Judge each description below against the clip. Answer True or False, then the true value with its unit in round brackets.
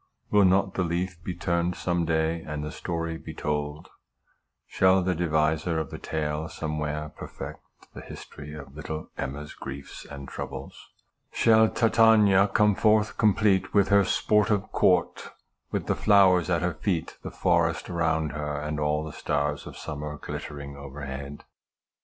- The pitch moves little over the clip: False (3.8 semitones)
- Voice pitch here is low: True (80 Hz)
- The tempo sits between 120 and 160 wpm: True (150 wpm)